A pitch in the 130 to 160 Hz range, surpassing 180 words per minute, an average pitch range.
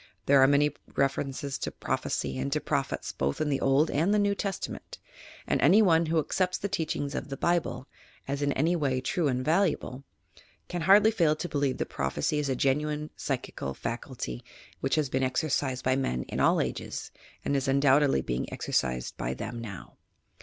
Yes: medium, 140 Hz; average, 190 wpm; average, 3.6 semitones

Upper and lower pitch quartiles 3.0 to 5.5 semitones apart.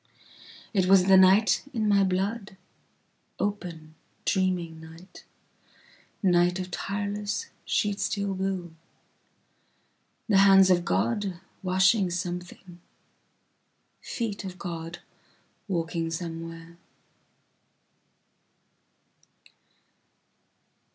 No: narrow, 2.5 semitones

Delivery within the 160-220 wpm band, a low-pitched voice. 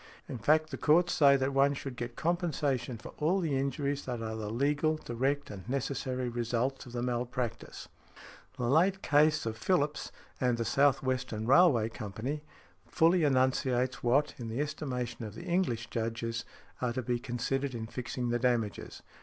Yes: average, 170 wpm; low, 130 Hz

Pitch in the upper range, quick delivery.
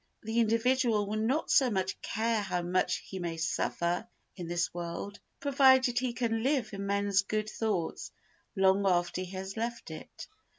No: high, 205 Hz; average, 165 wpm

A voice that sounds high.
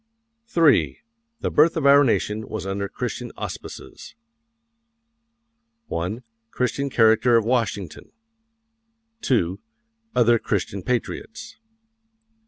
No: low, 115 Hz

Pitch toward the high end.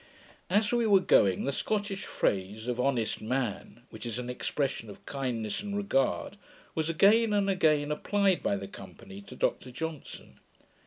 No: medium, 140 Hz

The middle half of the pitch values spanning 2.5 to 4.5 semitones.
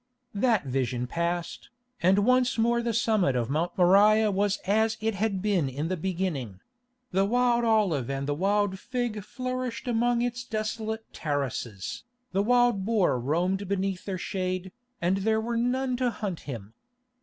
No: average, 4.9 semitones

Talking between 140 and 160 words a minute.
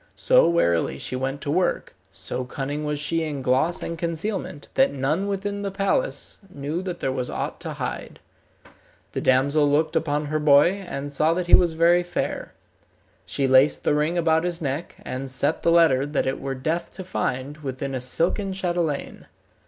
No: average, 185 wpm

